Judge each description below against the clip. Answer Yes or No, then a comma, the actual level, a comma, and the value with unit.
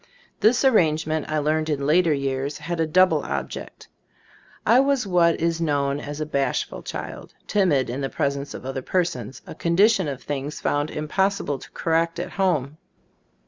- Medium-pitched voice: Yes, medium, 155 Hz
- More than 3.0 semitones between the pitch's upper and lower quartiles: Yes, average, 3.9 semitones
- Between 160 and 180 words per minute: Yes, average, 165 wpm